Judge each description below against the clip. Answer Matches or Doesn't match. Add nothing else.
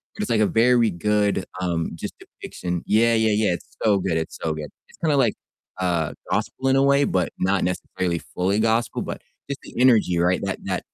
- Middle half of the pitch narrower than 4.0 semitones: Doesn't match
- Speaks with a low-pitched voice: Matches